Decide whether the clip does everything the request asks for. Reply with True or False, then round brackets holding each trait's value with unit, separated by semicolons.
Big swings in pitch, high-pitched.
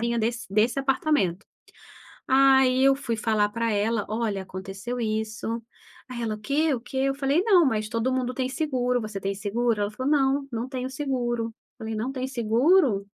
False (3.6 semitones; 240 Hz)